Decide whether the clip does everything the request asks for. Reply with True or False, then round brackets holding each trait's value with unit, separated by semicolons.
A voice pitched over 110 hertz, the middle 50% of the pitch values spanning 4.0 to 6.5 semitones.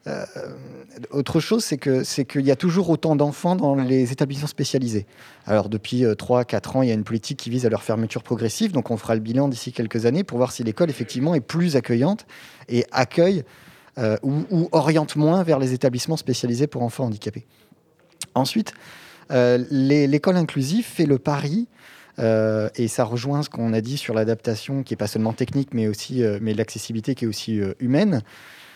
True (130 Hz; 4.6 semitones)